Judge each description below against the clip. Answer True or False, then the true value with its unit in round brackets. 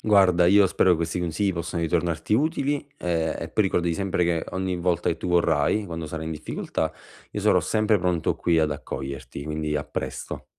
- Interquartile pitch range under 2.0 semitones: False (2.8 semitones)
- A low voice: True (85 Hz)